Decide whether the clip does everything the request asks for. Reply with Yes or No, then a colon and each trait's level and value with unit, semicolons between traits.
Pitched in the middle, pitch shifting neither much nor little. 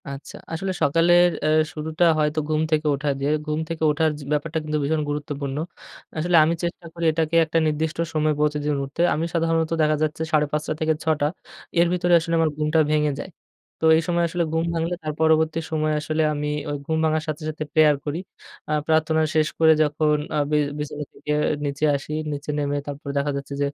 No: medium, 155 Hz; narrow, 1.4 semitones